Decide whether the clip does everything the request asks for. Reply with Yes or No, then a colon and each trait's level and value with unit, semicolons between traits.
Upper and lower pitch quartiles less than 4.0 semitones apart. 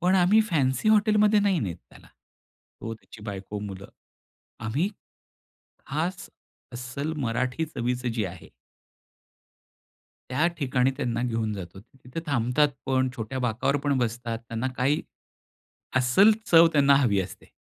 No: average, 5.0 semitones